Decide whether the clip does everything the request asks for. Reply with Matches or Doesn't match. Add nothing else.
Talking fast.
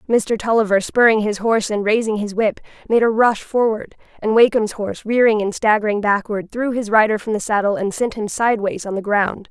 Matches